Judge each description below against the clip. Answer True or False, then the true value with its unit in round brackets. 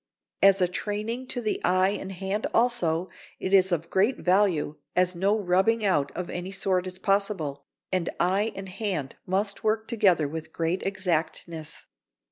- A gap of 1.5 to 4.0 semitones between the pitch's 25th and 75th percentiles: True (2.9 semitones)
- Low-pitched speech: False (190 Hz)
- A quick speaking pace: False (160 wpm)